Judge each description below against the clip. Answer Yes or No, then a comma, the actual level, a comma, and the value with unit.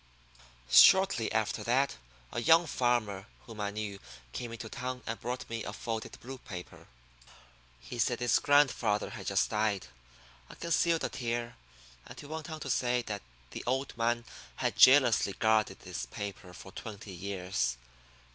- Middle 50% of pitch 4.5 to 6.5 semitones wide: No, average, 3.8 semitones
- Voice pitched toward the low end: Yes, low, 115 Hz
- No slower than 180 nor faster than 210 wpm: No, average, 155 wpm